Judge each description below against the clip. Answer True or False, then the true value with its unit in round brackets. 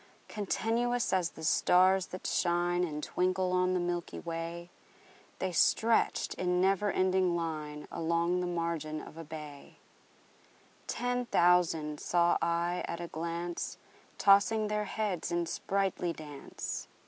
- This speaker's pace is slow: True (130 wpm)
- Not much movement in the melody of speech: True (2.1 semitones)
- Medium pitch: True (175 Hz)